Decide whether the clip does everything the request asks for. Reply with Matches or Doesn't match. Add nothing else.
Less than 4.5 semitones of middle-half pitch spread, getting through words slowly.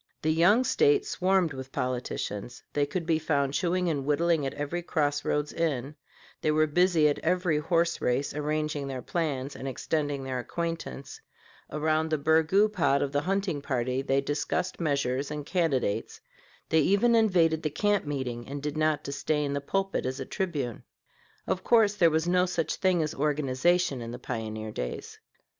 Doesn't match